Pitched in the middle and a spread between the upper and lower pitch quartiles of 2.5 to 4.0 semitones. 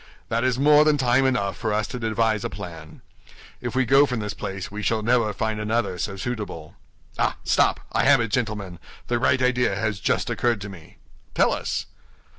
No: low, 110 Hz; average, 3.6 semitones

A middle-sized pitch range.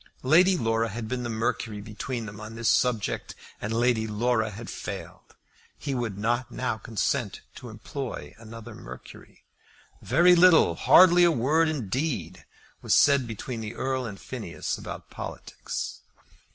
Yes: average, 3.3 semitones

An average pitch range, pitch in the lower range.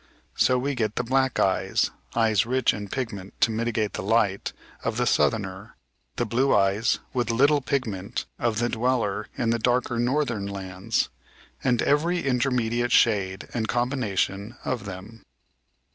Yes: average, 3.5 semitones; low, 115 Hz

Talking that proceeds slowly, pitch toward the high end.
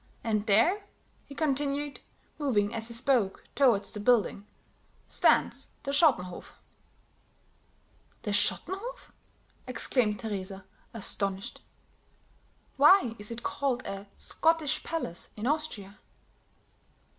Yes: slow, 100 wpm; high, 235 Hz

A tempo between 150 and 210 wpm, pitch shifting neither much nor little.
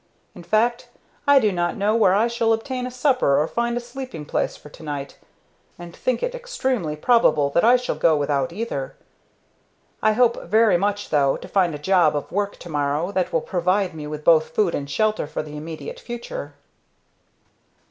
No: average, 190 wpm; wide, 7.4 semitones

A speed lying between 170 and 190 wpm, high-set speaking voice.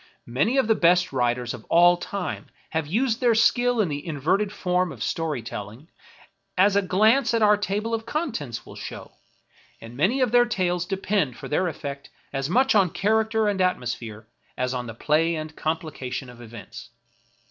No: average, 180 wpm; medium, 175 Hz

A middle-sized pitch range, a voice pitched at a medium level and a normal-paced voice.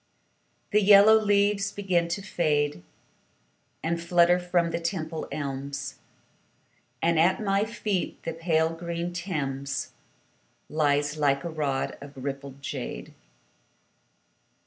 No: average, 4.3 semitones; medium, 165 Hz; slow, 110 wpm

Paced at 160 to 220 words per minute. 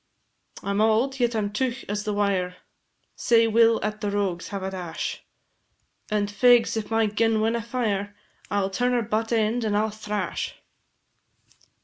Yes: average, 180 wpm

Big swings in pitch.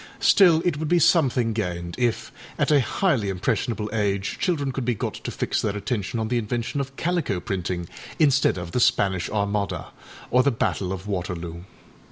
Yes: wide, 6.1 semitones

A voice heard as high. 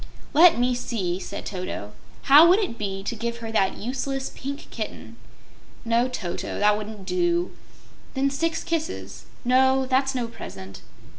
Yes: very high, 250 Hz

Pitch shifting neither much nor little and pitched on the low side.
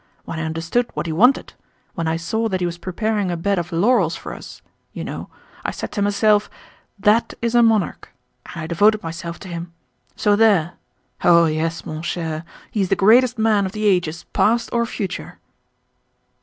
No: average, 4.5 semitones; high, 190 Hz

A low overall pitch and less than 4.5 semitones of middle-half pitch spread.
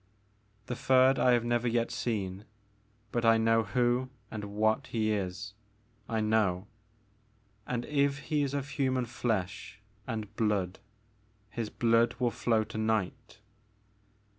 Yes: low, 115 Hz; narrow, 2.6 semitones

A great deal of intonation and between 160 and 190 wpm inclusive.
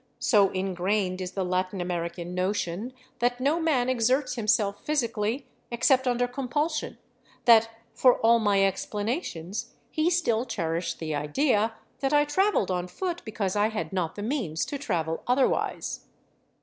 No: wide, 5.8 semitones; average, 145 wpm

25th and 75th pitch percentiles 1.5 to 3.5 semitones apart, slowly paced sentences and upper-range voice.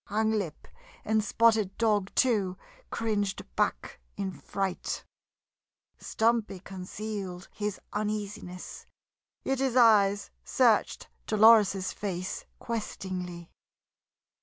Yes: narrow, 2.5 semitones; slow, 85 wpm; high, 205 Hz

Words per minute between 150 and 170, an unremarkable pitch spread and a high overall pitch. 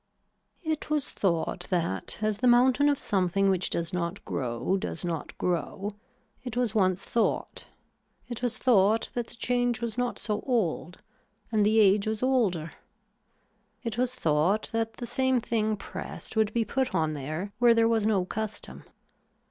Yes: average, 165 wpm; average, 4.7 semitones; high, 215 Hz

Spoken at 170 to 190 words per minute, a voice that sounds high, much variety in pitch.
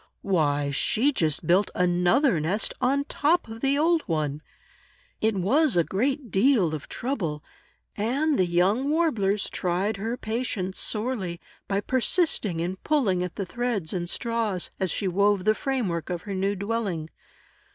No: average, 155 wpm; high, 200 Hz; wide, 5.9 semitones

